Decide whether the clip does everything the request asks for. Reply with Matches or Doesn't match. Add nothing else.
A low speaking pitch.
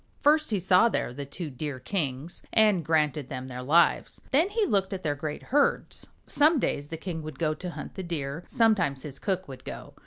Doesn't match